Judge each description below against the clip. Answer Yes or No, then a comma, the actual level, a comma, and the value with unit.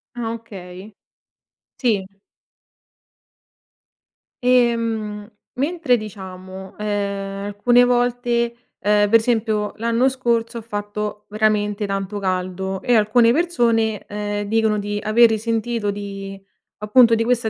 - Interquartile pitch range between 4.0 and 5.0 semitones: No, narrow, 2.4 semitones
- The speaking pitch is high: Yes, high, 215 Hz